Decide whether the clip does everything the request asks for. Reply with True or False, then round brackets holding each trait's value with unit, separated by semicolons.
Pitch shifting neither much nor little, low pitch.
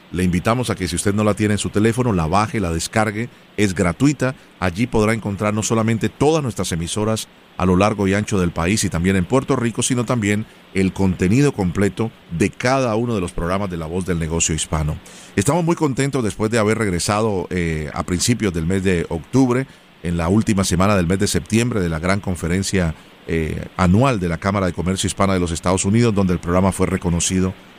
True (3.7 semitones; 100 Hz)